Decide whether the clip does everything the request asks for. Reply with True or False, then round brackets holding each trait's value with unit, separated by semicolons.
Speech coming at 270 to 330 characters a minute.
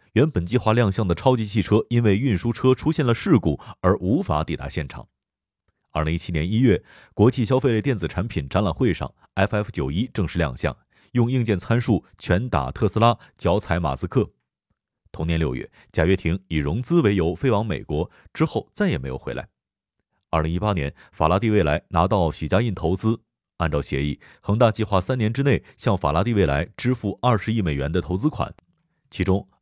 True (290 characters per minute)